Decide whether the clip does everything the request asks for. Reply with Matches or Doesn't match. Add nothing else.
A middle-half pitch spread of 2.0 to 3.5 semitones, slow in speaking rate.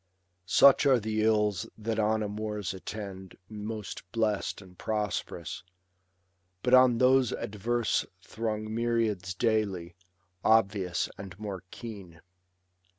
Matches